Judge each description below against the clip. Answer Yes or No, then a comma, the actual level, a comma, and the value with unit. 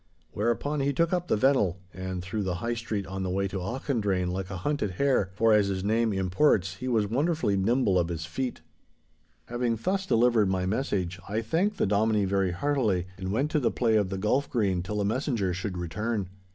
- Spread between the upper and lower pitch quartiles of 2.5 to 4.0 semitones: No, average, 4.8 semitones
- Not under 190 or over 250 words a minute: Yes, fast, 205 wpm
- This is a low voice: Yes, low, 105 Hz